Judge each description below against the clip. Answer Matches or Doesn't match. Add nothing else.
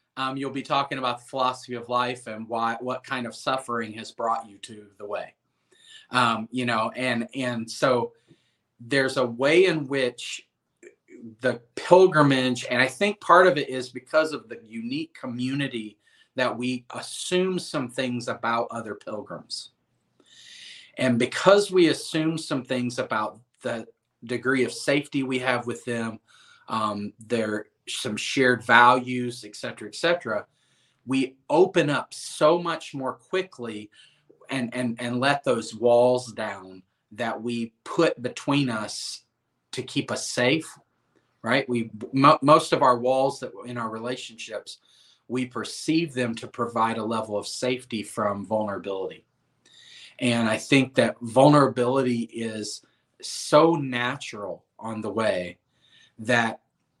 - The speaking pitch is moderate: Doesn't match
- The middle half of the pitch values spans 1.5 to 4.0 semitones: Matches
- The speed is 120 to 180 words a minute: Matches